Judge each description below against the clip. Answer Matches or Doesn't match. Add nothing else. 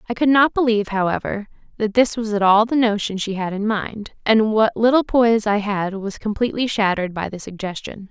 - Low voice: Doesn't match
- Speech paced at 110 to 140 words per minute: Doesn't match